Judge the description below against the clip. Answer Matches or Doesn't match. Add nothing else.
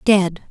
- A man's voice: Doesn't match